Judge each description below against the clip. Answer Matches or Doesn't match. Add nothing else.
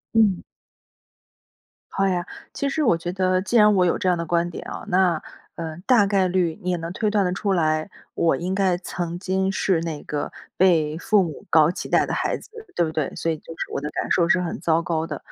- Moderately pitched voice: Matches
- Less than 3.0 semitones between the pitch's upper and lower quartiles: Matches